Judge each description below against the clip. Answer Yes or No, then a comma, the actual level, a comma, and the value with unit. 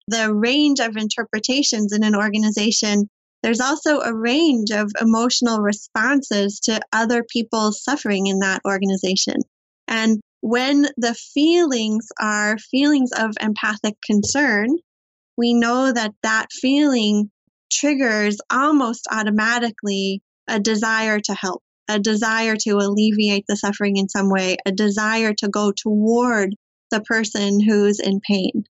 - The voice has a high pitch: Yes, high, 220 Hz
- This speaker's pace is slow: Yes, slow, 125 wpm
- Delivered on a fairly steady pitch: Yes, narrow, 2.3 semitones